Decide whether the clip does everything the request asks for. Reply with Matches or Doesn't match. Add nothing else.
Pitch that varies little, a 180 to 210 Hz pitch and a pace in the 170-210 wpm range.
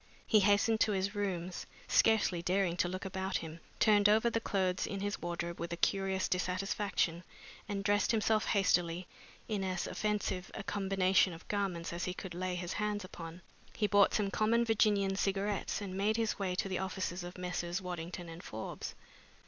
Matches